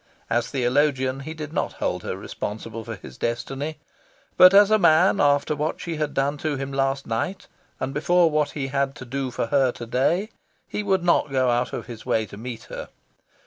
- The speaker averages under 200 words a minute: No, fast, 205 wpm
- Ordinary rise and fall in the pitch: Yes, average, 3.9 semitones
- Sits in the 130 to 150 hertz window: Yes, medium, 140 Hz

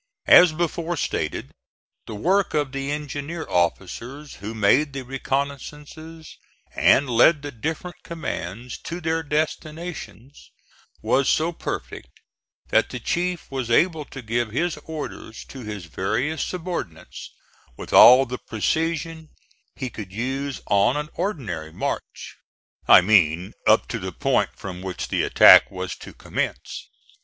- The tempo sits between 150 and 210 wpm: No, slow, 135 wpm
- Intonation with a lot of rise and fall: Yes, wide, 6.2 semitones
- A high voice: No, medium, 140 Hz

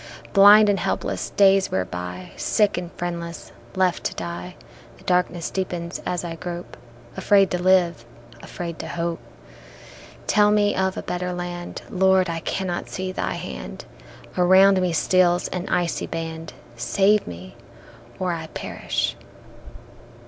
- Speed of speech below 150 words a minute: Yes, average, 140 wpm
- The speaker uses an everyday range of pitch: No, narrow, 2.2 semitones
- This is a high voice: No, medium, 175 Hz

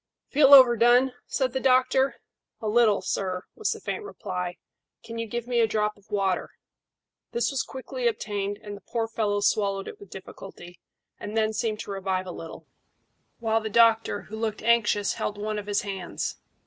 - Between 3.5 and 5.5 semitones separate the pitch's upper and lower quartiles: No, average, 2.9 semitones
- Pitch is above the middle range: Yes, high, 215 Hz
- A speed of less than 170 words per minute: No, average, 185 wpm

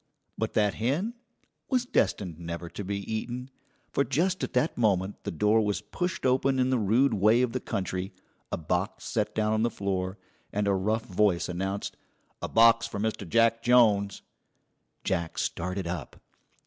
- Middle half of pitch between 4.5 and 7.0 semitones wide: No, average, 4.1 semitones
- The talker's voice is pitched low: Yes, low, 105 Hz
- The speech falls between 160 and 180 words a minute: Yes, average, 170 wpm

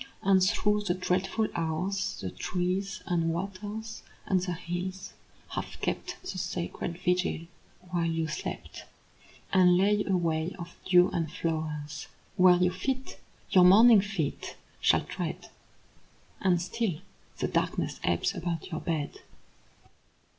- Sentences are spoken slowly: Yes, slow, 130 wpm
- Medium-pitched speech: Yes, medium, 180 Hz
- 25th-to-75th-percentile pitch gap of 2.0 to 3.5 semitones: Yes, narrow, 2.5 semitones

